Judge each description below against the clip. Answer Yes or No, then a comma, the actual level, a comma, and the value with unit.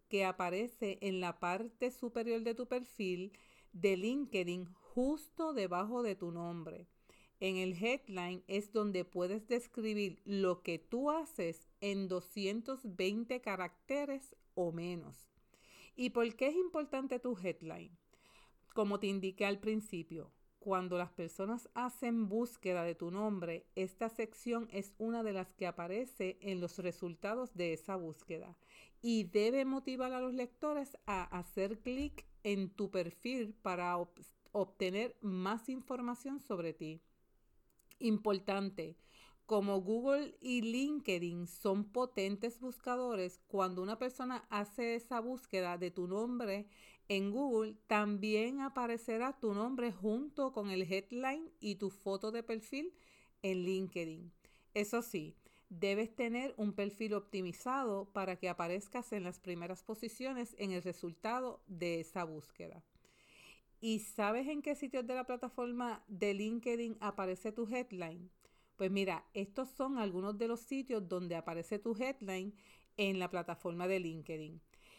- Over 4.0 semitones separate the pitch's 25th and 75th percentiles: Yes, average, 4.7 semitones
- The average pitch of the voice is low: No, high, 205 Hz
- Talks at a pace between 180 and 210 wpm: No, average, 135 wpm